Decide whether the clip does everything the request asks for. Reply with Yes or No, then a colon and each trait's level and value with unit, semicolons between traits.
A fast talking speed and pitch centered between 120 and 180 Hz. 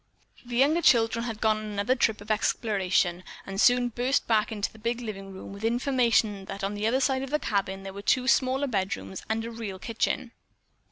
No: fast, 215 wpm; high, 220 Hz